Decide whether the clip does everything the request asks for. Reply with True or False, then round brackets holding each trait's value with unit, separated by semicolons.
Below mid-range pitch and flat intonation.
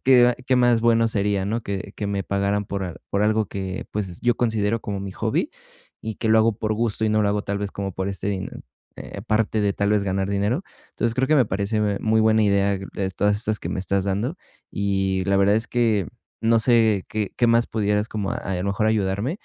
True (105 Hz; 2.1 semitones)